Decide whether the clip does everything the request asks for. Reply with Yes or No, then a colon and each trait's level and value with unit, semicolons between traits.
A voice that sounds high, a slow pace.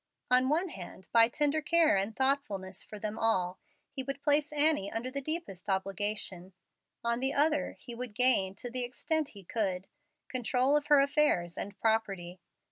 No: high, 240 Hz; average, 170 wpm